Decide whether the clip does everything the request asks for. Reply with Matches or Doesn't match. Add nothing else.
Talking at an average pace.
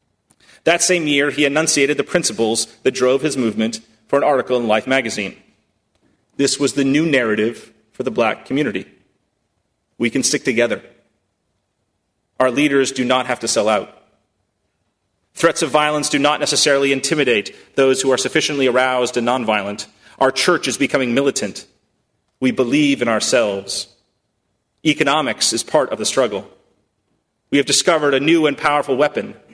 Matches